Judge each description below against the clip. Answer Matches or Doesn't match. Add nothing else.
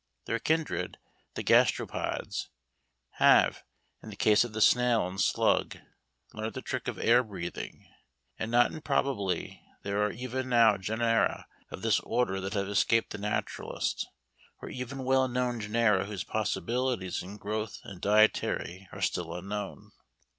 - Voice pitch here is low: Matches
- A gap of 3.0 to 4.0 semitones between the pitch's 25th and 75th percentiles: Matches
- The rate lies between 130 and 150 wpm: Matches